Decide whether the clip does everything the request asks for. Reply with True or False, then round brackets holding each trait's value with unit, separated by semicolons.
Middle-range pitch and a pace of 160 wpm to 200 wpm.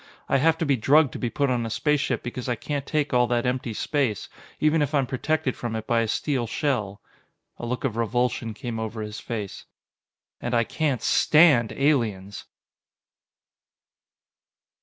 False (125 Hz; 170 wpm)